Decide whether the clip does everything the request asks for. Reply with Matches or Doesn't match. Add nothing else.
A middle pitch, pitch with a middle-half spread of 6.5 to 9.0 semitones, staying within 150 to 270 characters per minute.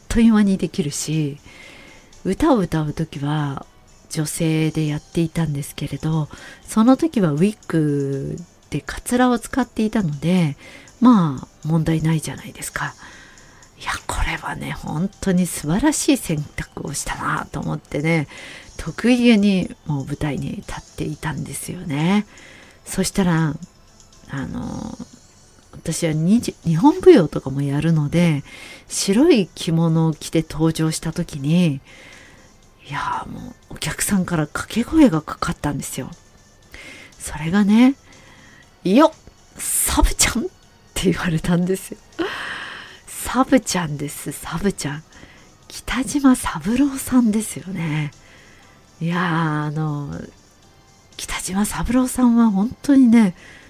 Doesn't match